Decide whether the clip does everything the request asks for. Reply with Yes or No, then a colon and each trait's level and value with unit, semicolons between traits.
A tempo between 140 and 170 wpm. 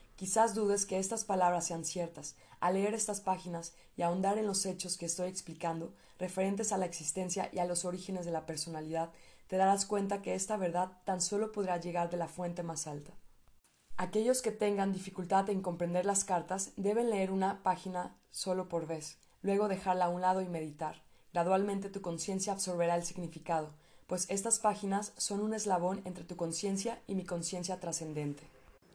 No: average, 180 wpm